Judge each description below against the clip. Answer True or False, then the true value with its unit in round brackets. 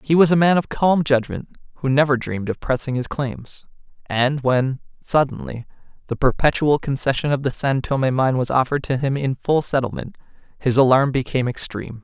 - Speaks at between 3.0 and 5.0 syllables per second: False (5.4 syllables/s)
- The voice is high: False (135 Hz)